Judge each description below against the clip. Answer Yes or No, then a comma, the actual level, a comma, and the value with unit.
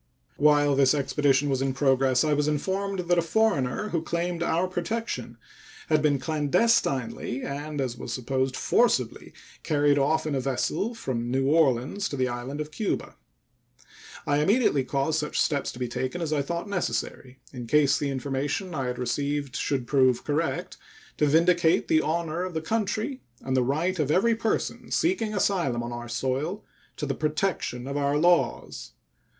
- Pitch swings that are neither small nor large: Yes, average, 4.4 semitones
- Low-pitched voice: No, medium, 145 Hz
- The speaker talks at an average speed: Yes, average, 170 wpm